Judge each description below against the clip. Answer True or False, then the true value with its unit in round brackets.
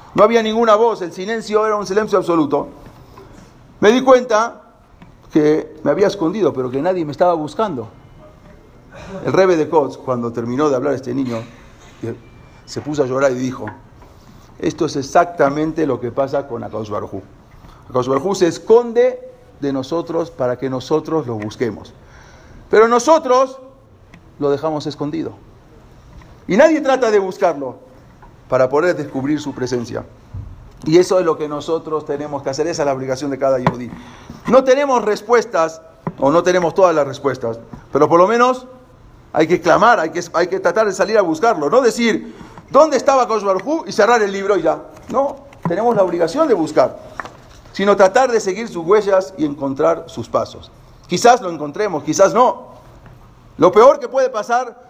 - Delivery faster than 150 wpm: True (165 wpm)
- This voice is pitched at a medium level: True (160 Hz)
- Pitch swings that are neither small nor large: False (8.2 semitones)